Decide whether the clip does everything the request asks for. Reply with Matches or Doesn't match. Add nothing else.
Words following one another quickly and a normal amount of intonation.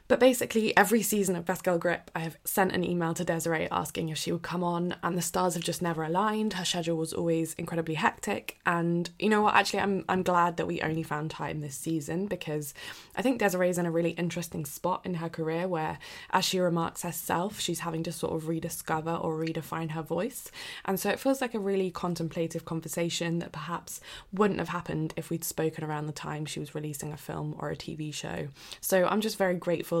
Doesn't match